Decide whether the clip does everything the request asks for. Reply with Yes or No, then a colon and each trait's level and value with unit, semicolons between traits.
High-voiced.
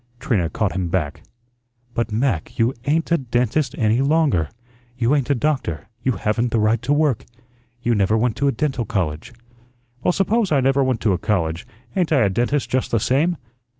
No: low, 120 Hz